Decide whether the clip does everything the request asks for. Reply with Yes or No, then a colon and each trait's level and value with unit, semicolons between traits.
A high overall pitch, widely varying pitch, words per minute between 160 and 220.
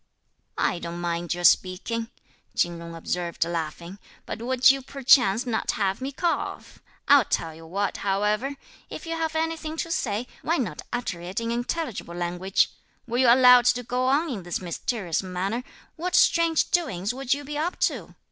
Yes: high, 230 Hz; wide, 7.4 semitones; average, 175 wpm